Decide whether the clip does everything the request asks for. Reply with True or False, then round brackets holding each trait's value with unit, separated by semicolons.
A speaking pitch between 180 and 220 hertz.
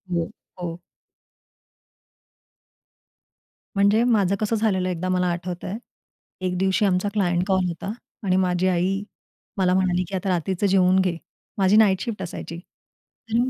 True (185 Hz)